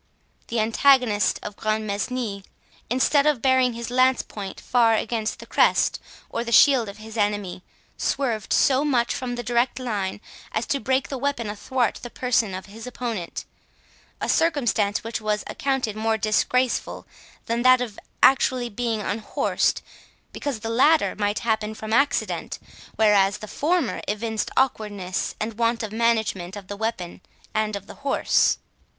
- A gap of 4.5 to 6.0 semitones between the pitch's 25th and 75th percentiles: No, average, 3.2 semitones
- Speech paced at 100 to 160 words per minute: Yes, average, 150 wpm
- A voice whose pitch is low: No, high, 230 Hz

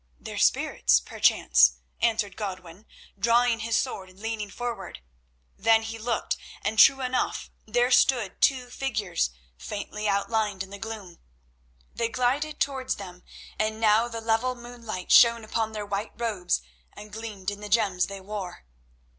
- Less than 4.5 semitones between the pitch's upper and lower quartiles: Yes, average, 2.9 semitones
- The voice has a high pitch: Yes, high, 220 Hz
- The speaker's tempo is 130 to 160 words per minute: Yes, average, 145 wpm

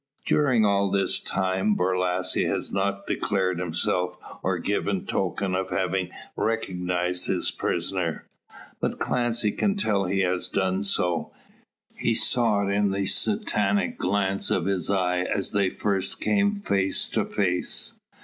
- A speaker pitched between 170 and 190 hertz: No, very low, 95 Hz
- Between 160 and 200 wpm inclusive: No, average, 140 wpm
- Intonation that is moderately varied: No, narrow, 2.0 semitones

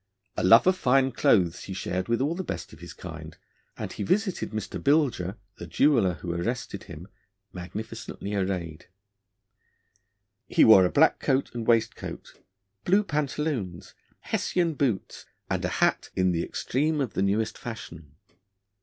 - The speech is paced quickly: No, average, 150 wpm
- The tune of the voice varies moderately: No, wide, 7.6 semitones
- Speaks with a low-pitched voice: Yes, low, 110 Hz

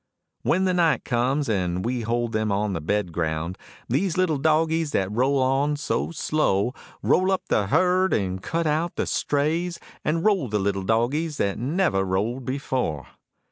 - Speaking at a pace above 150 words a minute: Yes, average, 170 wpm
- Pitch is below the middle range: Yes, low, 130 Hz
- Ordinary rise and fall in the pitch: No, wide, 7.9 semitones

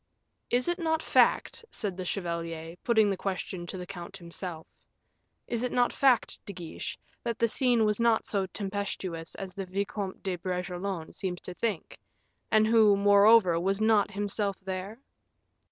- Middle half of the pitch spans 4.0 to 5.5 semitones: No, average, 3.4 semitones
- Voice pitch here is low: No, high, 200 Hz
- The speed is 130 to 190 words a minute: Yes, average, 160 wpm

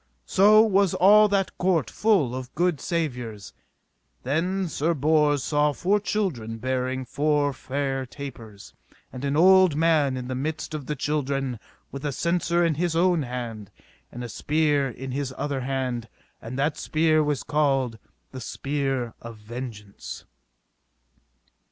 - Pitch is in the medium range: Yes, medium, 145 Hz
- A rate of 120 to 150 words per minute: Yes, average, 145 wpm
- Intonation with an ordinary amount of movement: Yes, average, 4.2 semitones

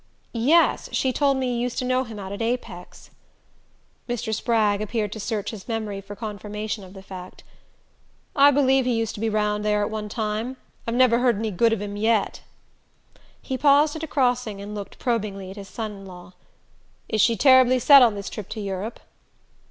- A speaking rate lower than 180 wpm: No, average, 200 wpm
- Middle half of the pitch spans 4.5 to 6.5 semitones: No, average, 3.4 semitones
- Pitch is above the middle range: Yes, high, 220 Hz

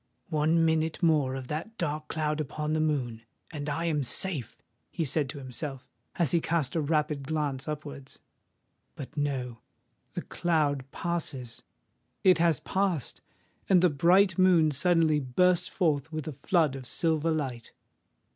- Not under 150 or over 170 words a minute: No, average, 140 wpm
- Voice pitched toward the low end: No, medium, 155 Hz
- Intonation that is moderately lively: Yes, average, 3.2 semitones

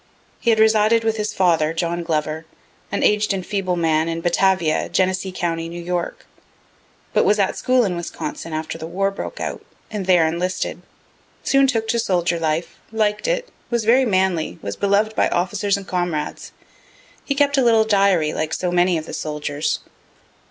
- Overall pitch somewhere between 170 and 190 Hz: Yes, medium, 185 Hz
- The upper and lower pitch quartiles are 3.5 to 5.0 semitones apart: Yes, average, 4.5 semitones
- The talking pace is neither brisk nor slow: Yes, average, 175 wpm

